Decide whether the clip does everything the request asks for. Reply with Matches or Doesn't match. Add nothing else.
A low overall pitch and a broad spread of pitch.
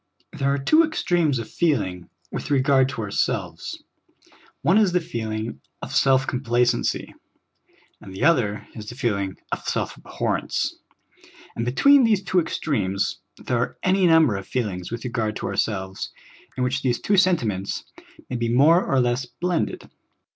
Matches